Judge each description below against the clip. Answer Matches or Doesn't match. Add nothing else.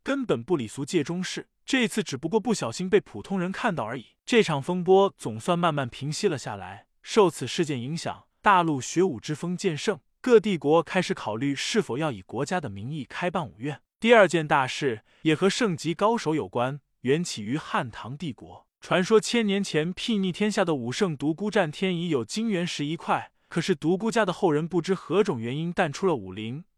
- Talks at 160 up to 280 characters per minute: Doesn't match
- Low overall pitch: Doesn't match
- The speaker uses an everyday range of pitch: Matches